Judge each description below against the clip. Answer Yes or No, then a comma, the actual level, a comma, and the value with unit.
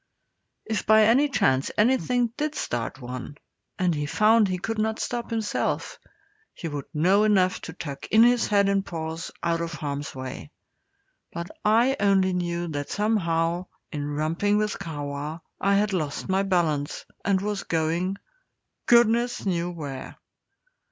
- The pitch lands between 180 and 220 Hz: Yes, medium, 185 Hz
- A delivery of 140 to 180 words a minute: Yes, average, 150 wpm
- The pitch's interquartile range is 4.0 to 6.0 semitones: Yes, average, 5.3 semitones